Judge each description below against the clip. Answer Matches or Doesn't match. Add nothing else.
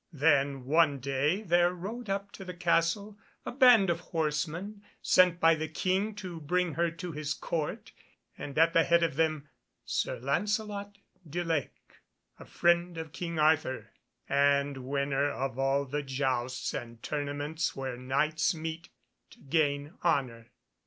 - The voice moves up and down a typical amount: Matches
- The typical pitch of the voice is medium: Matches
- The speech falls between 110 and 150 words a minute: Matches